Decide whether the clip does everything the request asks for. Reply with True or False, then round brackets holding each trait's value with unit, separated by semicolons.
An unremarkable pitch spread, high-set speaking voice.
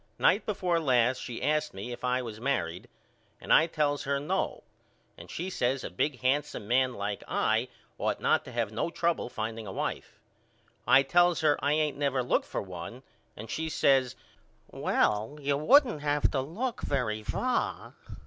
False (4.3 semitones; 135 Hz)